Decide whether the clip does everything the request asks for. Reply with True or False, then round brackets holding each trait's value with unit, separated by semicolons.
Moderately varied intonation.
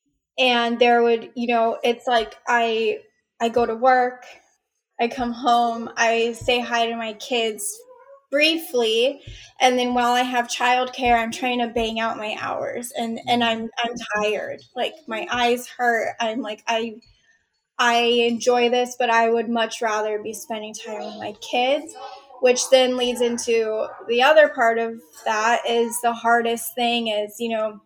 False (1.4 semitones)